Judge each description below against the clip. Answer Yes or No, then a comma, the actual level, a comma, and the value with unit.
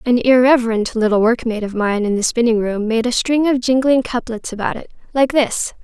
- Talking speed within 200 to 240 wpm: Yes, fast, 205 wpm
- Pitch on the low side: No, high, 235 Hz